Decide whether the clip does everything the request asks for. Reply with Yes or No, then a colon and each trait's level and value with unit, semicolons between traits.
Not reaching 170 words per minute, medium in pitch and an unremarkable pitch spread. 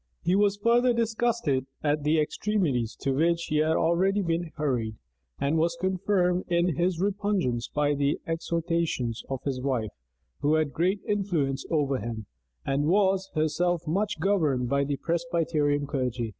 Yes: average, 150 wpm; medium, 160 Hz; average, 5.0 semitones